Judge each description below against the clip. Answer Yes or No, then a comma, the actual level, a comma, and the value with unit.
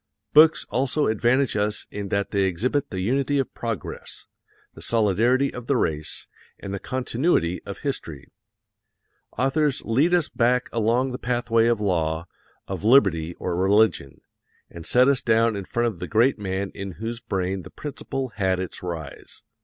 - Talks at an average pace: Yes, average, 160 wpm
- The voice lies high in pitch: No, low, 110 Hz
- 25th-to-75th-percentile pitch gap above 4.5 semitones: Yes, average, 5.2 semitones